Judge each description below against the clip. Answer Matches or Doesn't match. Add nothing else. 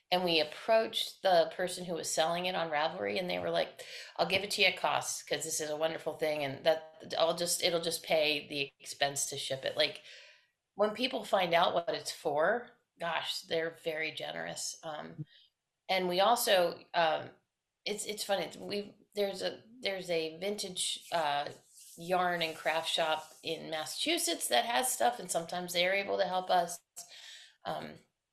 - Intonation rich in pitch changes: Doesn't match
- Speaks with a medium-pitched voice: Matches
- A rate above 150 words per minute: Matches